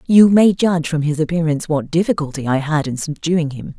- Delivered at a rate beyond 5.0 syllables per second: Yes, 5.7 syllables/s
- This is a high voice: No, medium, 160 Hz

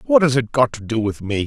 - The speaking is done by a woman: No, male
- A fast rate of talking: Yes, fast, 330 wpm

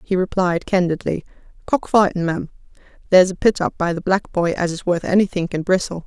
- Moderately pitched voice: Yes, medium, 180 Hz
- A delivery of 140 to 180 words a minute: No, average, 200 wpm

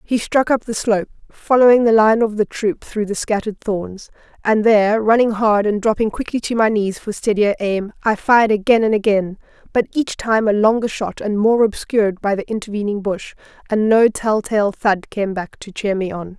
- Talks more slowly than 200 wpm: No, fast, 205 wpm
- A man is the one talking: No, female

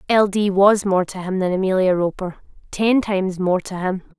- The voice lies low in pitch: No, high, 190 Hz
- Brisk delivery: No, average, 185 wpm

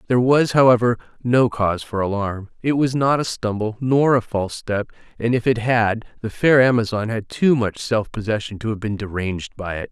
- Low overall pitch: Yes, low, 115 Hz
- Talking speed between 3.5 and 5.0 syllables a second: No, 5.3 syllables/s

